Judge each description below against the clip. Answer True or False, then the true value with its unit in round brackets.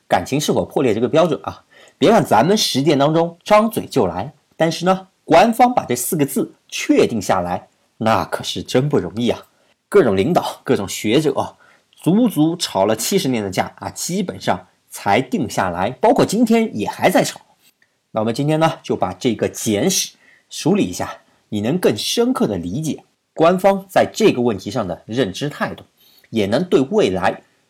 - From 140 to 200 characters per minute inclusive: False (260 characters per minute)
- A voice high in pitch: False (180 Hz)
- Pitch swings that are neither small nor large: False (7.1 semitones)